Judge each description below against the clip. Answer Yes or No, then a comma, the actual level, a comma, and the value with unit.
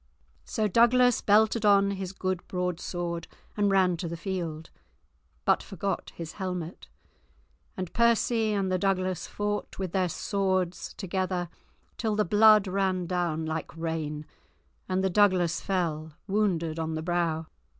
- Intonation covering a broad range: No, average, 3.0 semitones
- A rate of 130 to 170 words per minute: Yes, average, 140 wpm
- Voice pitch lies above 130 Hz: Yes, medium, 185 Hz